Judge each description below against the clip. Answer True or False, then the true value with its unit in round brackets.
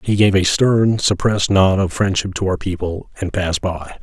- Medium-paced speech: False (210 wpm)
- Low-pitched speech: True (95 Hz)